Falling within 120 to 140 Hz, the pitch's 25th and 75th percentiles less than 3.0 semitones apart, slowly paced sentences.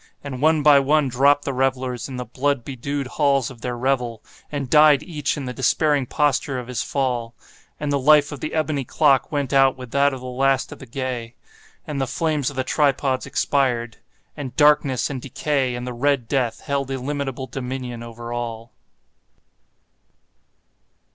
No: low, 135 Hz; narrow, 2.4 semitones; average, 175 wpm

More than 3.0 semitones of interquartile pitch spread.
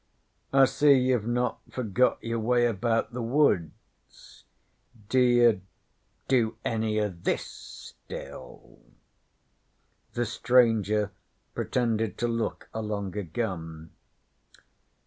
No: average, 2.7 semitones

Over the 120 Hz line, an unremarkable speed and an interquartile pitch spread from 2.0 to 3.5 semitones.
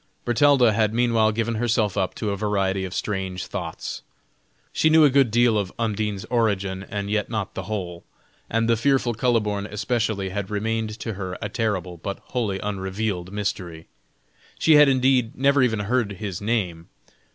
No: low, 105 Hz; average, 165 wpm; average, 3.2 semitones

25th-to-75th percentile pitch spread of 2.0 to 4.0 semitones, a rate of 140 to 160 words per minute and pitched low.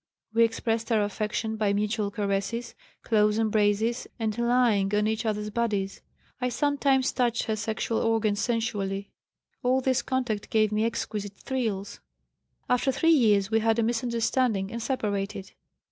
No: narrow, 2.4 semitones; average, 145 wpm; high, 220 Hz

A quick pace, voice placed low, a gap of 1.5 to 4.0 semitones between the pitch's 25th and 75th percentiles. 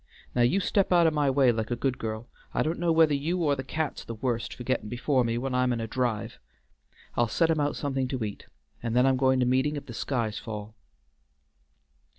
Yes: fast, 230 wpm; low, 130 Hz; average, 3.6 semitones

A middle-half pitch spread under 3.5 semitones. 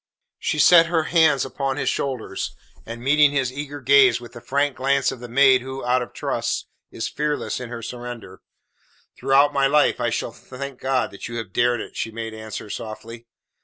Yes: average, 3.0 semitones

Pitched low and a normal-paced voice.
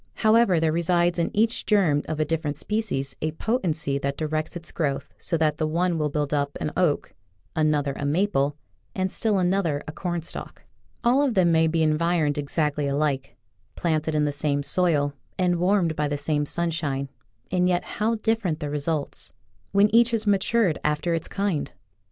No: medium, 160 Hz; average, 180 wpm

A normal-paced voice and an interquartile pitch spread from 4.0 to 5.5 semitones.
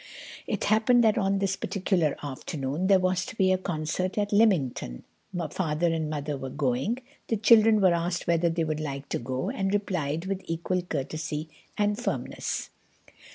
Yes: average, 160 wpm; average, 4.6 semitones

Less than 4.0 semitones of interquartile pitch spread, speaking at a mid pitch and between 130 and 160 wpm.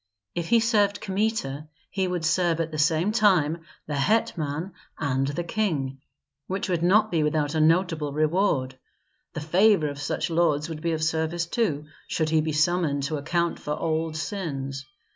No: average, 3.4 semitones; medium, 160 Hz; average, 170 wpm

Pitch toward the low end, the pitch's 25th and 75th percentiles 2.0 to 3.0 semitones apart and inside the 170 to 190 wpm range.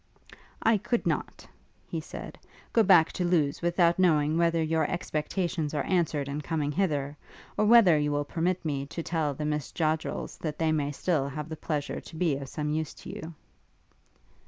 No: medium, 155 Hz; average, 2.7 semitones; average, 180 wpm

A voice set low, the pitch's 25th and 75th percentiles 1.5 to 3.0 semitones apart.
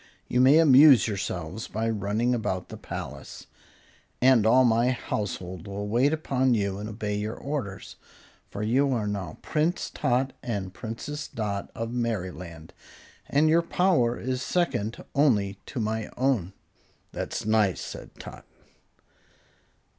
No: low, 115 Hz; average, 4.3 semitones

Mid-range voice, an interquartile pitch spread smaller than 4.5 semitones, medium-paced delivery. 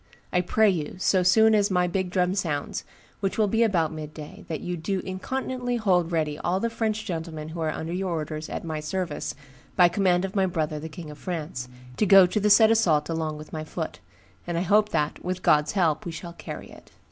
No: medium, 180 Hz; average, 3.7 semitones; fast, 220 wpm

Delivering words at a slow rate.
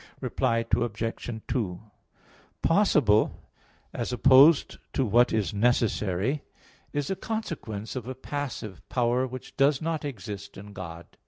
Yes: slow, 120 wpm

